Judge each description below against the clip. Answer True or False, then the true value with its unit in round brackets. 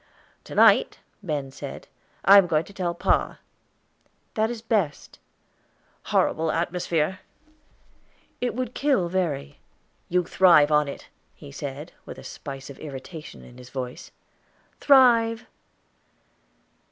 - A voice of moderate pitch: True (170 Hz)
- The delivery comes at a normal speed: False (120 wpm)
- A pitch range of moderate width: False (5.8 semitones)